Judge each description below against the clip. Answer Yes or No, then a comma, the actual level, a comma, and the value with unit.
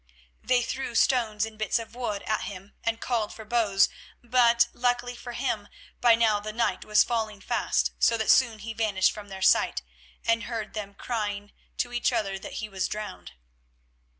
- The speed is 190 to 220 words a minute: No, average, 180 wpm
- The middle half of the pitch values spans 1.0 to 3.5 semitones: Yes, narrow, 2.4 semitones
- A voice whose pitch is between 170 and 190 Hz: No, high, 220 Hz